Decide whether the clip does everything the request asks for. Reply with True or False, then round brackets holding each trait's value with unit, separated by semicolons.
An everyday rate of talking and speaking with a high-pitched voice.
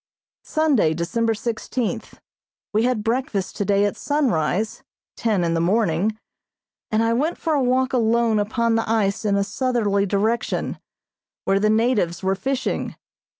True (145 wpm; 220 Hz)